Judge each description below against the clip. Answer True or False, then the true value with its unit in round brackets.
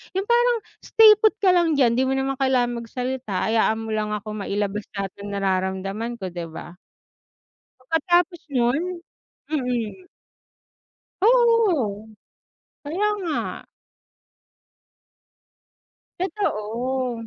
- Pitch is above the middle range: True (250 Hz)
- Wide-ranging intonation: True (8.5 semitones)